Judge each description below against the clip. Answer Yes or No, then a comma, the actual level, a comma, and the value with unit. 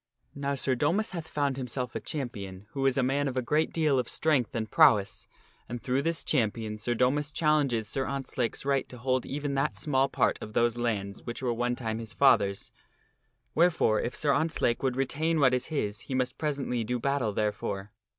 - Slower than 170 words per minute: No, average, 200 wpm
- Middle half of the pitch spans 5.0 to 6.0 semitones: No, average, 3.6 semitones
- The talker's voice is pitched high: No, low, 130 Hz